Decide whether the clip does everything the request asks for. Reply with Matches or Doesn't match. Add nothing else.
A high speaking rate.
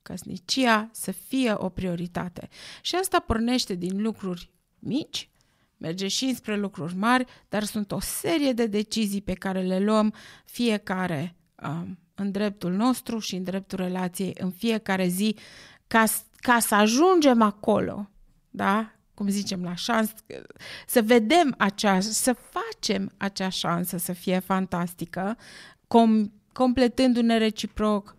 Doesn't match